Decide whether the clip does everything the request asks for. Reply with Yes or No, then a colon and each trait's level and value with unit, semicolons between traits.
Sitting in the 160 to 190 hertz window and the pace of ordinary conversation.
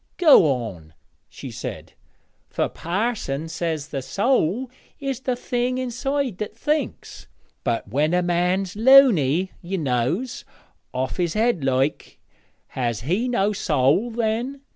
No: medium, 185 Hz; slow, 125 wpm